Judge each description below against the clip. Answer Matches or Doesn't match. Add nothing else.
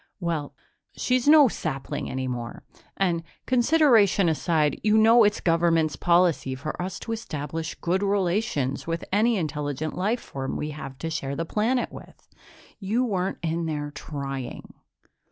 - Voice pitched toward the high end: Doesn't match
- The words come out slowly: Doesn't match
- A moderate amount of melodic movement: Doesn't match